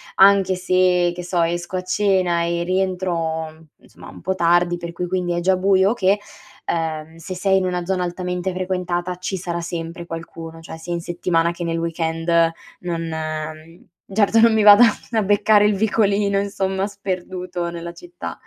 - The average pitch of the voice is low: No, medium, 180 Hz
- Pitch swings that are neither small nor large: No, narrow, 2.1 semitones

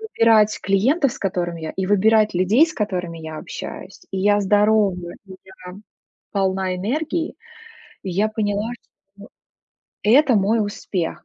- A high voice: Yes, high, 205 Hz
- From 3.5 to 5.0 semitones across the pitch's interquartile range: No, narrow, 2.6 semitones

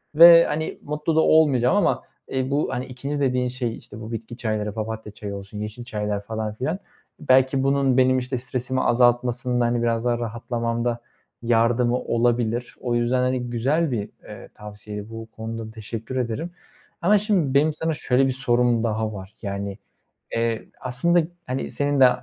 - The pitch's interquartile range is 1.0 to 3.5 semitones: Yes, average, 2.8 semitones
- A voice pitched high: No, low, 120 Hz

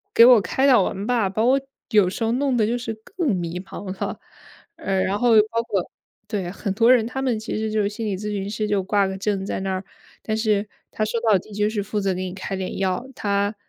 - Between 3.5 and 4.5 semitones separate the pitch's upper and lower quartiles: No, average, 2.9 semitones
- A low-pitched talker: No, high, 210 Hz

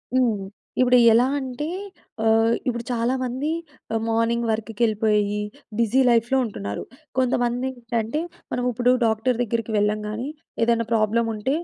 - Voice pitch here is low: No, high, 230 Hz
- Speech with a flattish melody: Yes, narrow, 2.0 semitones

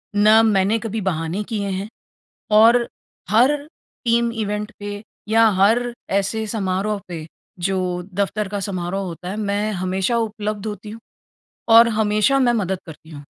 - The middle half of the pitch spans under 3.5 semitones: Yes, narrow, 2.6 semitones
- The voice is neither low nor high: No, high, 210 Hz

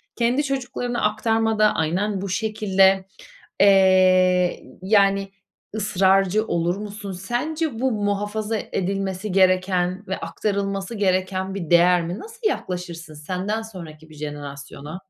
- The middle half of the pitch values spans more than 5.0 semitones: No, average, 2.9 semitones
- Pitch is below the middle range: No, high, 195 Hz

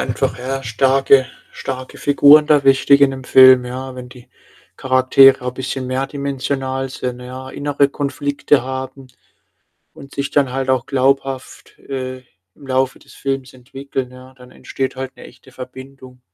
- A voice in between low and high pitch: No, low, 130 Hz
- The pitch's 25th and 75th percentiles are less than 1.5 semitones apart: Yes, narrow, 1.1 semitones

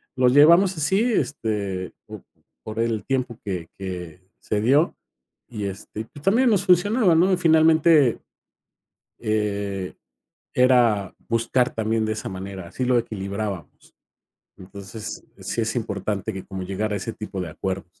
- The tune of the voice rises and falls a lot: Yes, wide, 5.8 semitones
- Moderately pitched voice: No, low, 110 Hz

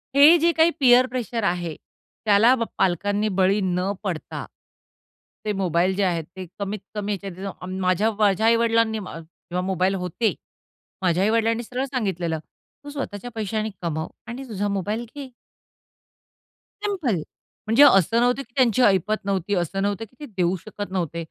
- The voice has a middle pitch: No, high, 205 Hz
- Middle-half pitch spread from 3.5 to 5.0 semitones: Yes, average, 4.0 semitones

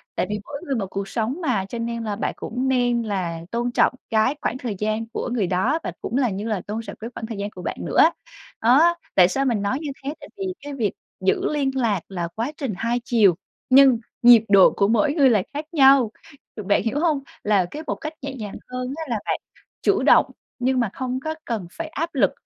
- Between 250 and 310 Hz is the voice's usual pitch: No, high, 235 Hz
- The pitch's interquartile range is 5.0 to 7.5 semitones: No, average, 4.5 semitones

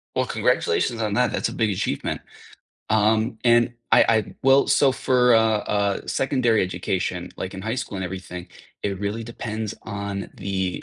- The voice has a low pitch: Yes, low, 110 Hz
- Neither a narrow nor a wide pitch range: Yes, average, 3.1 semitones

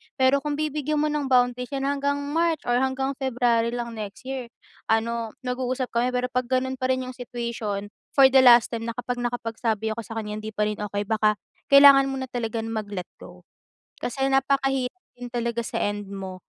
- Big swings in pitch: No, average, 2.9 semitones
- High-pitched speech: Yes, high, 245 Hz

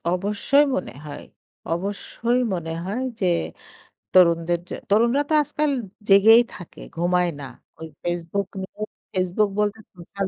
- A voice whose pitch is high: Yes, high, 195 Hz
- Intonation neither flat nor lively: Yes, average, 3.6 semitones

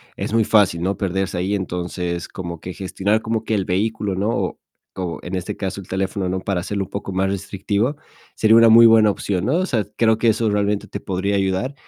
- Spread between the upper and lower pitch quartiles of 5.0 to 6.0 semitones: No, average, 2.8 semitones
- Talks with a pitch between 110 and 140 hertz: No, low, 100 Hz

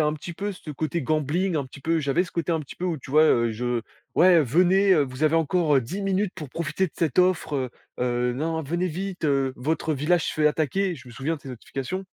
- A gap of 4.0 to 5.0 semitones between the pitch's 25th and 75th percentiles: Yes, average, 4.7 semitones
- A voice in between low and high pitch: Yes, medium, 155 Hz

